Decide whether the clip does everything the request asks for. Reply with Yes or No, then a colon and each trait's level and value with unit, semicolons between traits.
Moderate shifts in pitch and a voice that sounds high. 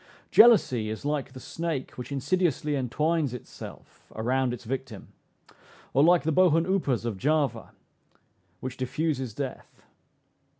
No: average, 4.2 semitones; low, 135 Hz